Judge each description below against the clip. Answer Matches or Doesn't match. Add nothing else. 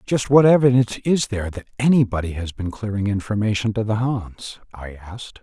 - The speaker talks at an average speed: Matches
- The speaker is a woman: Doesn't match